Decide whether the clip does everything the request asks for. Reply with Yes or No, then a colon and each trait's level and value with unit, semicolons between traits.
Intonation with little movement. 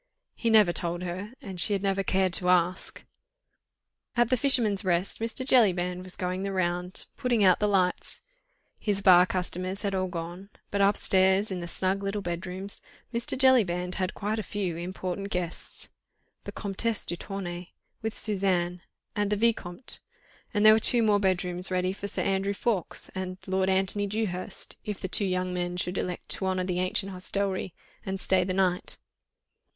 Yes: narrow, 2.0 semitones